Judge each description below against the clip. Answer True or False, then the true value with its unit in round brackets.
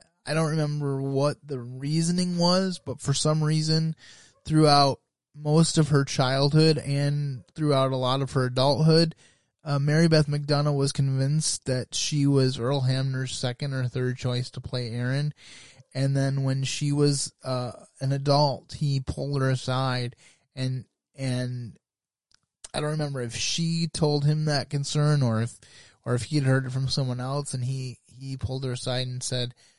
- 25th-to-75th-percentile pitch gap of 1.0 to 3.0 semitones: True (2.6 semitones)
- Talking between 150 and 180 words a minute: True (165 wpm)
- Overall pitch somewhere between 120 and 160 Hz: True (135 Hz)